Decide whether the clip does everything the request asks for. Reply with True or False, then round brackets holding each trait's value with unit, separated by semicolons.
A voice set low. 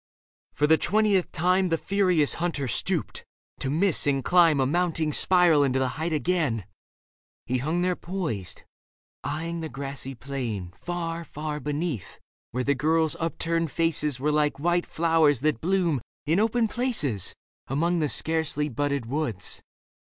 False (155 Hz)